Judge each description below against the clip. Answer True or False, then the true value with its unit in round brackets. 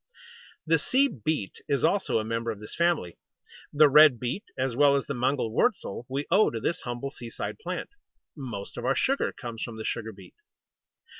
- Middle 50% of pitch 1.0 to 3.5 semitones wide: False (5.0 semitones)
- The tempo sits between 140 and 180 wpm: False (190 wpm)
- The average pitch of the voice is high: False (130 Hz)